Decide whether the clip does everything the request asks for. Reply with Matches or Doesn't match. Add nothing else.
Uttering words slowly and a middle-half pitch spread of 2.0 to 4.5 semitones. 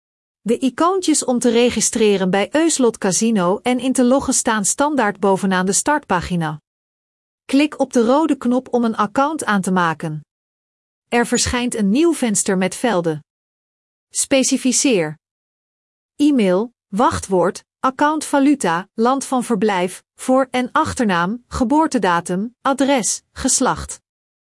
Doesn't match